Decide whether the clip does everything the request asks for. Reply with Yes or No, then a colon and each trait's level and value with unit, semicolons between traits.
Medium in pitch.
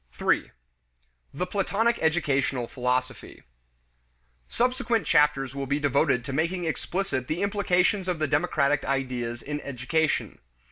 Yes: medium, 150 Hz